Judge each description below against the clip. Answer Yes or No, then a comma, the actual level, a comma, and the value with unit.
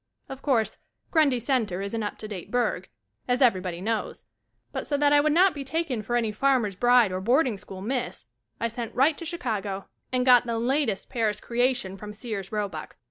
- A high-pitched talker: Yes, high, 235 Hz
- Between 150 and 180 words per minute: No, average, 195 wpm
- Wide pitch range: No, average, 4.3 semitones